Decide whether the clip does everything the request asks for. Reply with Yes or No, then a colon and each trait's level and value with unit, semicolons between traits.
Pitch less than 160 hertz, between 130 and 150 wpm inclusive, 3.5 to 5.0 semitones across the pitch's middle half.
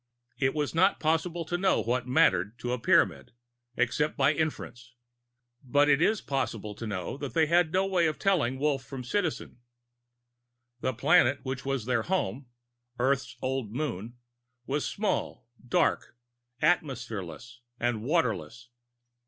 Yes: low, 135 Hz; average, 140 wpm; average, 4.7 semitones